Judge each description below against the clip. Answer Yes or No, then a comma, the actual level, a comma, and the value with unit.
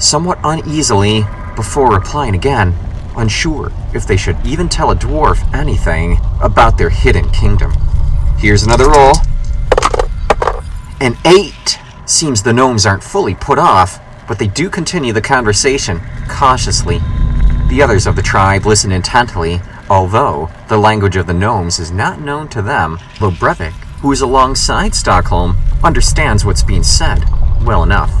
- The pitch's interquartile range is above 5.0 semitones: Yes, wide, 5.4 semitones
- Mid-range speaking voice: No, low, 105 Hz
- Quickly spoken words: No, average, 145 wpm